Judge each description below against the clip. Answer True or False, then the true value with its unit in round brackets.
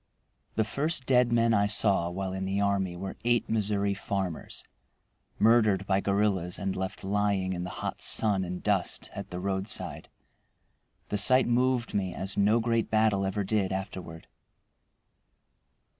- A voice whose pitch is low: True (100 Hz)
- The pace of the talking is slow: False (150 wpm)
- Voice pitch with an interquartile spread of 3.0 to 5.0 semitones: False (2.5 semitones)